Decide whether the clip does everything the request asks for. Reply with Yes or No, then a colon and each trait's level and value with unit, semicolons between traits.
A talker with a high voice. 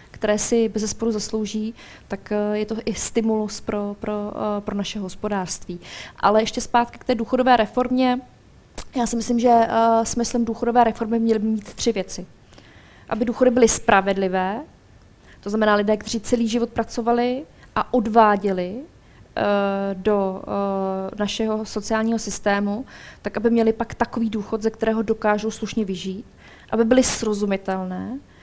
Yes: high, 220 Hz